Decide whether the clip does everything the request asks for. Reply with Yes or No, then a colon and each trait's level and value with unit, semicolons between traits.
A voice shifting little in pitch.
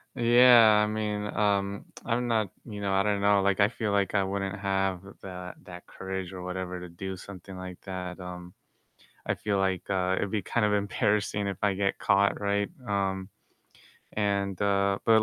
Yes: narrow, 1.6 semitones